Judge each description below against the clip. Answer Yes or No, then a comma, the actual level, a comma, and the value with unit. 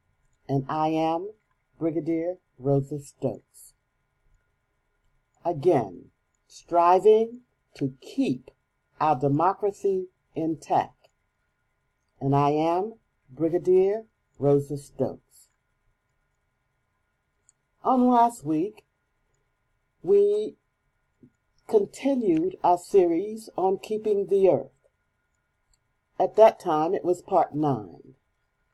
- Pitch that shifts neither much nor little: No, wide, 7.7 semitones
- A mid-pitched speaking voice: Yes, medium, 165 Hz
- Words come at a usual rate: No, slow, 75 wpm